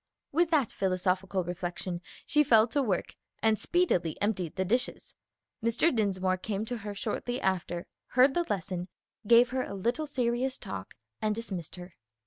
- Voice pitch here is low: No, high, 210 Hz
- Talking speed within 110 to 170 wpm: Yes, average, 155 wpm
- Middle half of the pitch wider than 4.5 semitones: Yes, average, 5.1 semitones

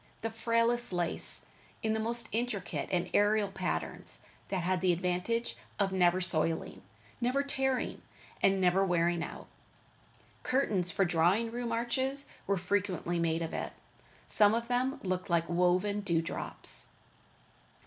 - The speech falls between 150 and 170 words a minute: No, average, 140 wpm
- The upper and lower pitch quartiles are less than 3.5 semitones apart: No, average, 4.7 semitones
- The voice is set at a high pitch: Yes, high, 195 Hz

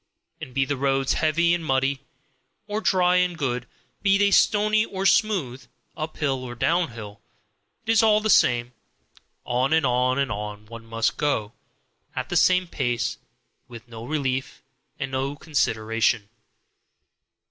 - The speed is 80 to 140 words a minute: Yes, slow, 135 wpm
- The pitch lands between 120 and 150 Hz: Yes, low, 135 Hz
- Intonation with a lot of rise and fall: Yes, wide, 6.3 semitones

